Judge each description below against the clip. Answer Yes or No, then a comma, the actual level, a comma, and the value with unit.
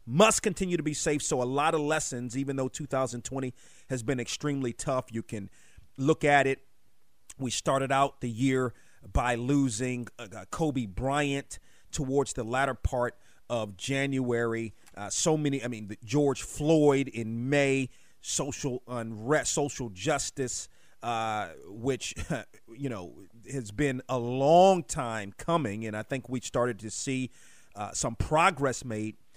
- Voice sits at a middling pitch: No, low, 130 Hz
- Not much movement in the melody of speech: No, average, 3.4 semitones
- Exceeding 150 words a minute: No, average, 145 wpm